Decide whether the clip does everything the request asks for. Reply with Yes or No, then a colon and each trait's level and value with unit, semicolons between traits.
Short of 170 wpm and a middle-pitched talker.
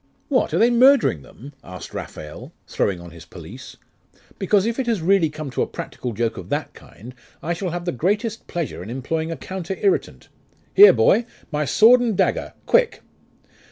No: average, 185 wpm; medium, 175 Hz